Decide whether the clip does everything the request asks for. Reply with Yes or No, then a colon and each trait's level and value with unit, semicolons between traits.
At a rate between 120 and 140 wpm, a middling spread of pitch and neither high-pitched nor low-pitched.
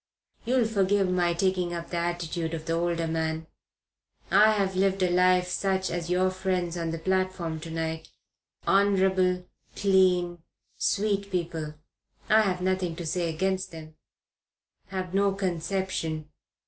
No: slow, 135 wpm; narrow, 2.3 semitones; medium, 180 Hz